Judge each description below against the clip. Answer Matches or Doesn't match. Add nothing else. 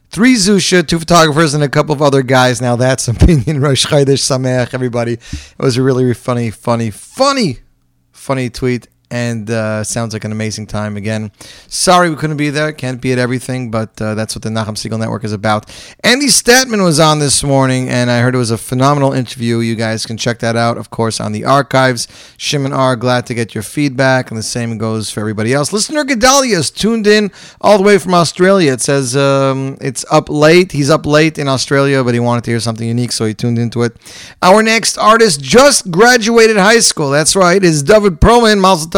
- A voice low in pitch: Matches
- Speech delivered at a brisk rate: Matches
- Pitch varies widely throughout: Matches